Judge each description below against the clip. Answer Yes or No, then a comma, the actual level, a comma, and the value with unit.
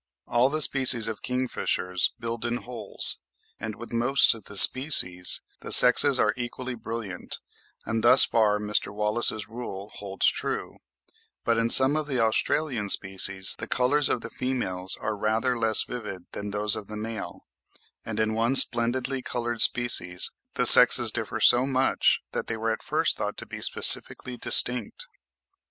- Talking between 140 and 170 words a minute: Yes, average, 160 wpm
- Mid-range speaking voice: No, low, 115 Hz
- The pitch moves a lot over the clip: No, average, 3.0 semitones